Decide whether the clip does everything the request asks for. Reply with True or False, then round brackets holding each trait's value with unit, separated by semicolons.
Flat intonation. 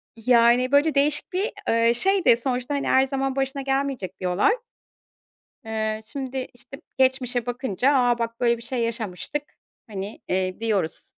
False (3.1 semitones)